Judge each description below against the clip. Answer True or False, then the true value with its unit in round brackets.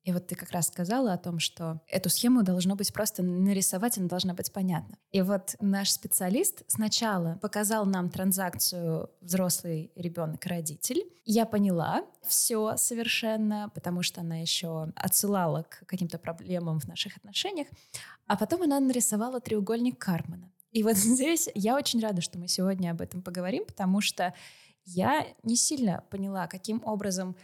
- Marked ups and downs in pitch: False (3.7 semitones)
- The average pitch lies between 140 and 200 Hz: True (190 Hz)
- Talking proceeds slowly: False (155 wpm)